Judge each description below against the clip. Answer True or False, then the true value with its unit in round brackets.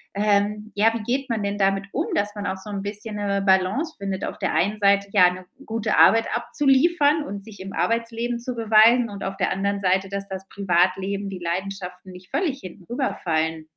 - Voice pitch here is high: True (200 Hz)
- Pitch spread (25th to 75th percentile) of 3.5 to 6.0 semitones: False (2.9 semitones)